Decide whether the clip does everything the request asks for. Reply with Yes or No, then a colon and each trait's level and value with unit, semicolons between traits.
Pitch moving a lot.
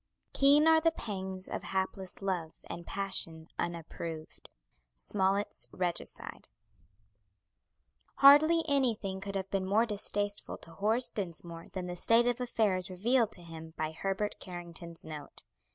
No: average, 4.4 semitones